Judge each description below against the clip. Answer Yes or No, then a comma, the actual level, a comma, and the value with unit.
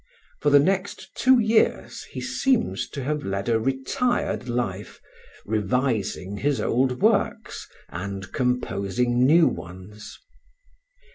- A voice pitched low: Yes, low, 125 Hz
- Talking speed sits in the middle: No, slow, 115 wpm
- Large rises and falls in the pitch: Yes, wide, 6.3 semitones